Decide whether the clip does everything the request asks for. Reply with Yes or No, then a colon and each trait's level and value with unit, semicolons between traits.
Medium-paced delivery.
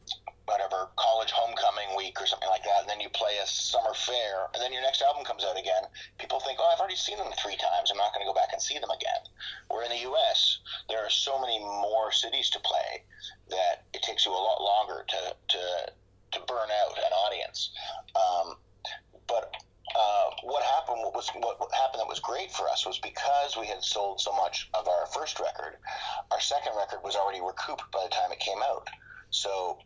No: fast, 215 wpm